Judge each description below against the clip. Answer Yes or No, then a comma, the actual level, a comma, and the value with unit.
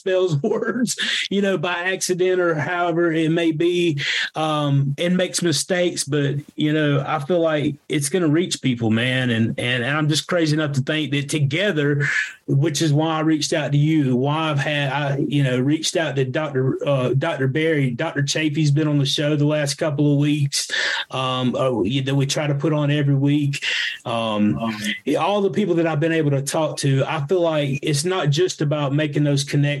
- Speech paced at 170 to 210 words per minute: Yes, average, 200 wpm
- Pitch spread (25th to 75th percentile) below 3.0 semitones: Yes, narrow, 2.6 semitones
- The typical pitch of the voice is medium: Yes, medium, 150 Hz